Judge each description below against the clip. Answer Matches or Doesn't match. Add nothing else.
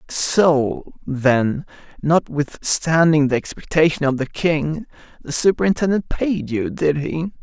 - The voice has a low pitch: Doesn't match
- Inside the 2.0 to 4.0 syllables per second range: Matches